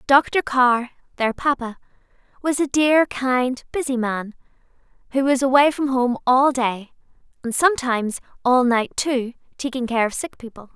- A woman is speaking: Yes, female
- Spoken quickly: No, average, 150 wpm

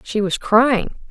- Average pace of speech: Yes, average, 165 wpm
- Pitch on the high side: Yes, high, 220 Hz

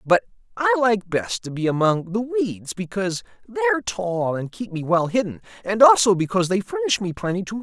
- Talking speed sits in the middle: No, fast, 215 wpm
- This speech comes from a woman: No, male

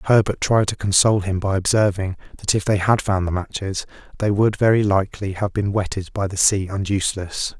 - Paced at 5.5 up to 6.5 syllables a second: Yes, 5.6 syllables/s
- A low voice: Yes, low, 100 Hz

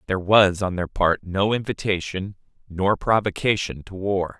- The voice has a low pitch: Yes, very low, 95 Hz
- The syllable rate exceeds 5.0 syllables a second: No, 4.7 syllables/s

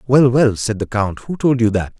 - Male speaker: Yes, male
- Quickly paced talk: Yes, fast, 270 wpm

